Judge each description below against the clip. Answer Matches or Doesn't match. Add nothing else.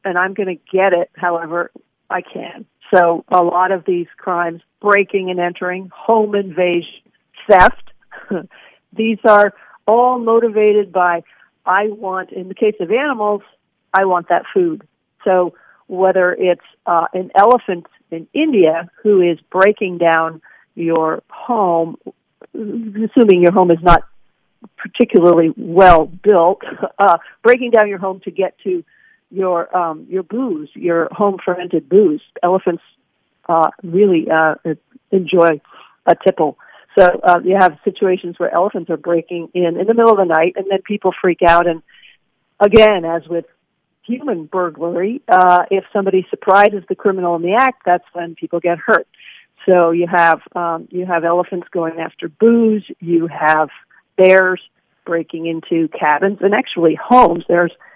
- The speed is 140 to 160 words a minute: Matches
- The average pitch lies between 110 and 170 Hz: Doesn't match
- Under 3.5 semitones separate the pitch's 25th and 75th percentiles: Matches